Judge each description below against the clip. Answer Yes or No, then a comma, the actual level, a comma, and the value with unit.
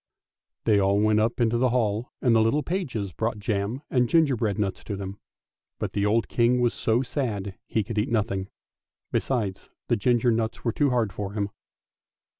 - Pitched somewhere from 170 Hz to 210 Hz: No, low, 110 Hz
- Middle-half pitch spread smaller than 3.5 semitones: Yes, average, 3.1 semitones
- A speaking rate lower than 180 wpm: No, average, 190 wpm